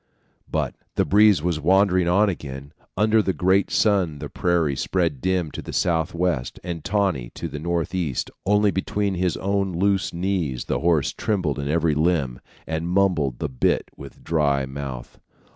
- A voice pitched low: Yes, very low, 85 Hz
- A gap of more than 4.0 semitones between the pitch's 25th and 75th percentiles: Yes, average, 4.4 semitones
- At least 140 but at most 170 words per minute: Yes, average, 160 wpm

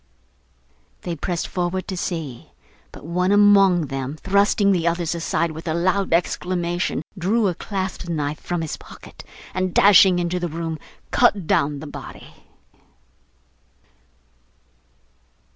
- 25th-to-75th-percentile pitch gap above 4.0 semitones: No, narrow, 2.5 semitones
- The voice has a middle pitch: Yes, medium, 175 Hz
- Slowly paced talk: Yes, slow, 125 wpm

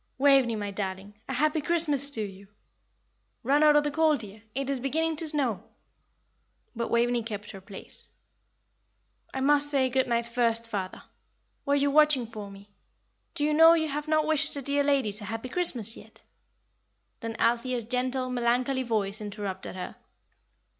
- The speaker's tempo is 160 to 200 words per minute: Yes, average, 165 wpm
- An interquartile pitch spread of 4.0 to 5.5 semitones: Yes, average, 4.8 semitones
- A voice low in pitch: No, very high, 255 Hz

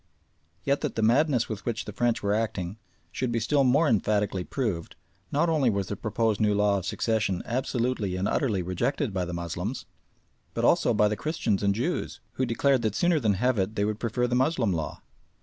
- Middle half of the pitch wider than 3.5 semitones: Yes, average, 4.1 semitones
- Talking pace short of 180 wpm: No, average, 200 wpm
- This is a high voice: No, low, 110 Hz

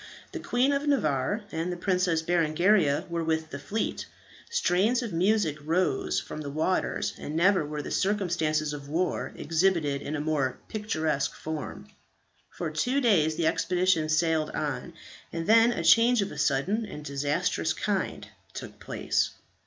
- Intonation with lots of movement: No, average, 4.4 semitones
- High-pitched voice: No, medium, 165 Hz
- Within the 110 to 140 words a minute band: No, average, 155 wpm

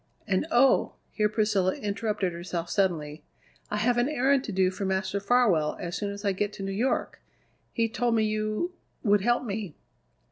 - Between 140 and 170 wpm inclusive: No, average, 180 wpm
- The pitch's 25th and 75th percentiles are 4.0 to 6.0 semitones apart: No, average, 3.3 semitones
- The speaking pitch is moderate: No, high, 205 Hz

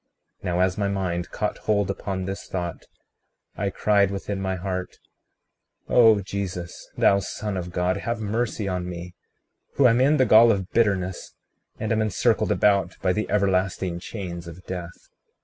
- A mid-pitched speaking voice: No, very low, 95 Hz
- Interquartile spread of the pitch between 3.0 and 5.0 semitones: No, narrow, 2.5 semitones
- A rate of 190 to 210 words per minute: No, average, 165 wpm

